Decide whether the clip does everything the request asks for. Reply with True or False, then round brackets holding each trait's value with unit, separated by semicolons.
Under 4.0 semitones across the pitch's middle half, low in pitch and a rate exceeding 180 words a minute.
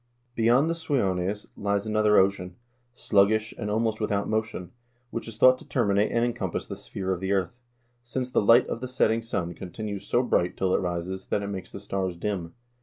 True (3.5 semitones; 105 Hz; 200 wpm)